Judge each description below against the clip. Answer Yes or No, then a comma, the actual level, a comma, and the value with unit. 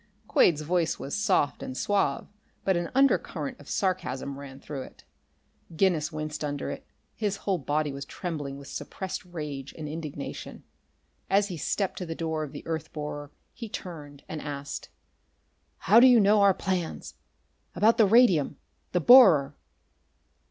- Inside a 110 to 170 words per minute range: Yes, average, 155 wpm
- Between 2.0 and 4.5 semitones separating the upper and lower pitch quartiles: No, average, 4.9 semitones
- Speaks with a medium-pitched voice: Yes, medium, 160 Hz